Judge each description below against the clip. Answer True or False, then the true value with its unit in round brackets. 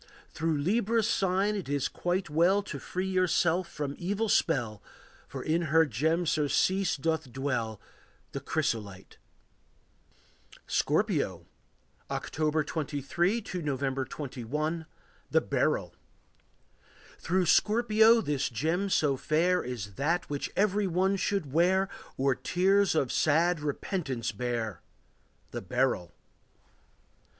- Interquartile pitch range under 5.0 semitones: False (5.3 semitones)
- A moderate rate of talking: False (110 wpm)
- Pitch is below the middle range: False (160 Hz)